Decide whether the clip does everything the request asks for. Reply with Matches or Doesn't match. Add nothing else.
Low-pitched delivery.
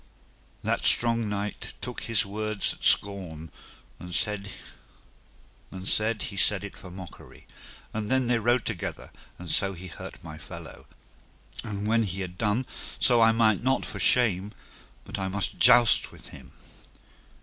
Matches